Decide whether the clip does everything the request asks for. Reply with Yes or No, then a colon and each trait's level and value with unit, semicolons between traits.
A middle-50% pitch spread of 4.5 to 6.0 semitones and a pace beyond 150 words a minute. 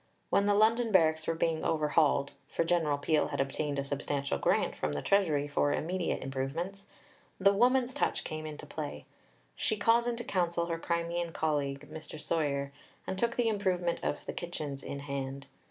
Yes: average, 4.9 semitones; average, 170 wpm